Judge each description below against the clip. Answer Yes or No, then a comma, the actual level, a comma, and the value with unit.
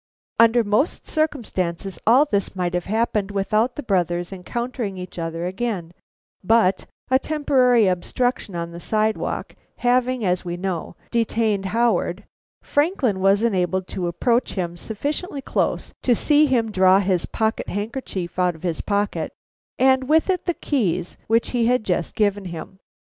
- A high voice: Yes, high, 210 Hz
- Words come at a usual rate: Yes, average, 150 wpm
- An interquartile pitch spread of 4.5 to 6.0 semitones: Yes, average, 5.0 semitones